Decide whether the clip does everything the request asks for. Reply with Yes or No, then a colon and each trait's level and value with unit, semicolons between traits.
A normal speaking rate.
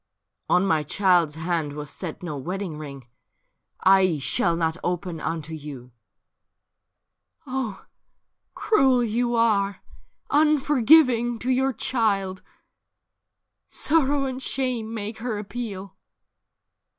No: slow, 110 wpm